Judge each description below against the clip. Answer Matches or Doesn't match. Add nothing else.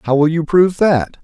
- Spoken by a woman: Doesn't match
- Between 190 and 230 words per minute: Doesn't match